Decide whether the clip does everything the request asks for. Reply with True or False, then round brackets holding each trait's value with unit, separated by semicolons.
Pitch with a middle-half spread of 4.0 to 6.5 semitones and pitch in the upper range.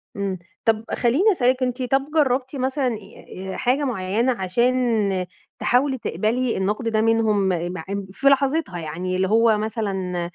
True (4.9 semitones; 225 Hz)